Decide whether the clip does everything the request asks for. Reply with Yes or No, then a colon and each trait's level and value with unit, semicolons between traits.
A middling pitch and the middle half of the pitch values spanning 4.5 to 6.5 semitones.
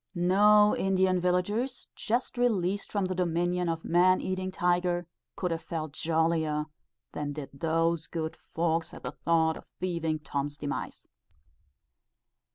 No: medium, 175 Hz; narrow, 2.5 semitones